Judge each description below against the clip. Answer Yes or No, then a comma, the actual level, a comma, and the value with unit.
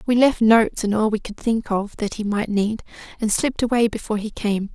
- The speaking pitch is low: No, high, 215 Hz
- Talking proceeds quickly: Yes, fast, 240 wpm